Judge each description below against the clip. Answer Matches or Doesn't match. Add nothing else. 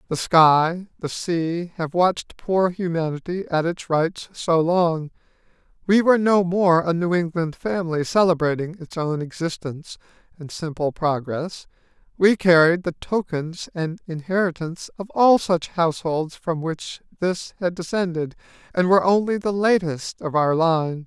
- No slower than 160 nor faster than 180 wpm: Doesn't match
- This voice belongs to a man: Matches